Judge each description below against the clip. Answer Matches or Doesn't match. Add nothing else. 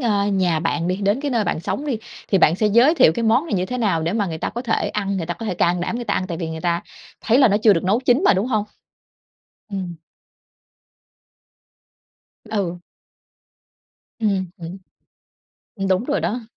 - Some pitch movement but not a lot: Matches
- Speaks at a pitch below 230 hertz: Matches